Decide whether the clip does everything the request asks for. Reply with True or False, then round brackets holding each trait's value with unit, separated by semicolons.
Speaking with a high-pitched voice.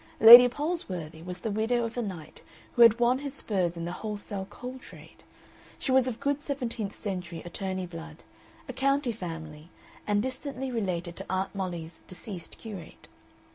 True (205 Hz)